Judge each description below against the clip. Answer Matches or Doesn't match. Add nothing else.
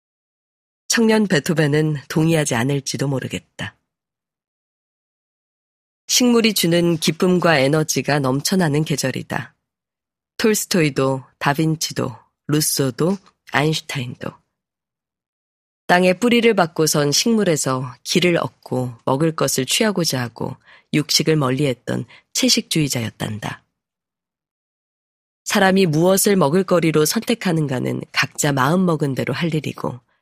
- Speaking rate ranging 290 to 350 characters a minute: Doesn't match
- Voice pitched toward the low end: Doesn't match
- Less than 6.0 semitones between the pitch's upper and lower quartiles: Matches